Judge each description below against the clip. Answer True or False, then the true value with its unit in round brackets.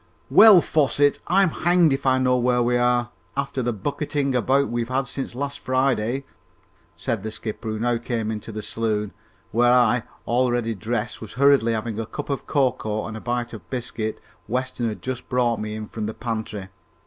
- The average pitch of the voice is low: True (120 Hz)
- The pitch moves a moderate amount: True (3.1 semitones)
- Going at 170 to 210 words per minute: True (185 wpm)